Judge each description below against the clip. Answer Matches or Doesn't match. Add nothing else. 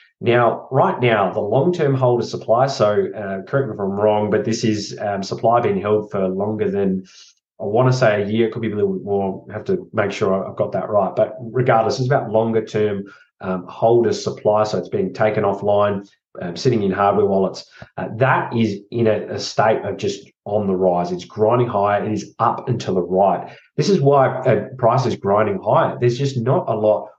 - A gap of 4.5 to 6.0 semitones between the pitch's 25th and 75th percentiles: Doesn't match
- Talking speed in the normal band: Doesn't match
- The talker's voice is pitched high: Doesn't match